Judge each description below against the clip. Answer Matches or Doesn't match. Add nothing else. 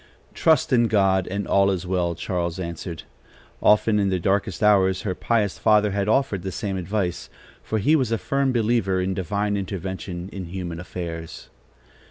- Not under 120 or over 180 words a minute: Matches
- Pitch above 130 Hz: Doesn't match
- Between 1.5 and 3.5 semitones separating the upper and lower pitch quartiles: Matches